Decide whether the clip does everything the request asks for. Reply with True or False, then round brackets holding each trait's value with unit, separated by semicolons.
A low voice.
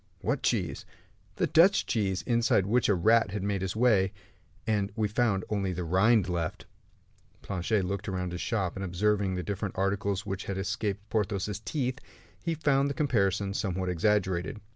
True (100 Hz)